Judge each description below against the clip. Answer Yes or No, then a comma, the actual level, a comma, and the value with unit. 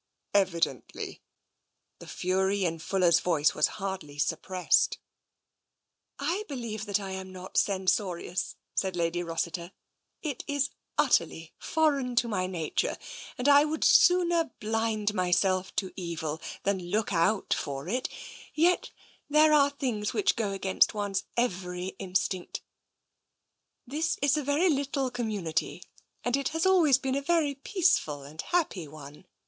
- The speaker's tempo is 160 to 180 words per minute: No, average, 140 wpm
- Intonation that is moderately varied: No, wide, 7.8 semitones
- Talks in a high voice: Yes, high, 200 Hz